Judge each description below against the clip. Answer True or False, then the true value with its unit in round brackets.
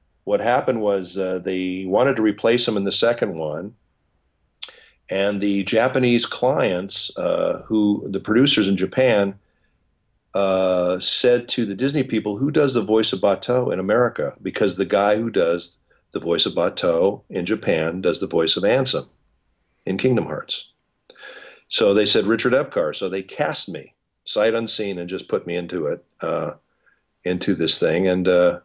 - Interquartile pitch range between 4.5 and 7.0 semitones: False (3.8 semitones)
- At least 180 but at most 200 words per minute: False (165 wpm)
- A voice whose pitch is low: True (100 Hz)